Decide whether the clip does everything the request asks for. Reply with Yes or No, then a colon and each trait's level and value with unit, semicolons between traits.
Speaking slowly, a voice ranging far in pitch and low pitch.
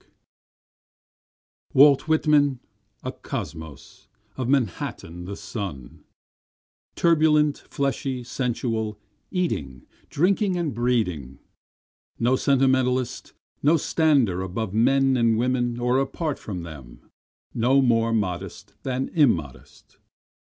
Yes: slow, 95 wpm; wide, 5.7 semitones; low, 125 Hz